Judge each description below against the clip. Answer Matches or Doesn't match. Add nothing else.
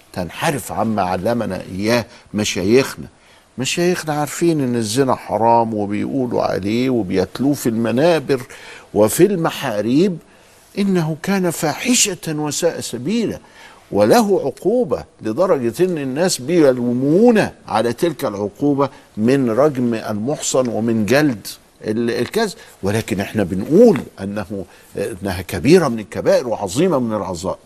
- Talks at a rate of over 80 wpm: Matches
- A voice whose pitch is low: Matches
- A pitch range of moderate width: Doesn't match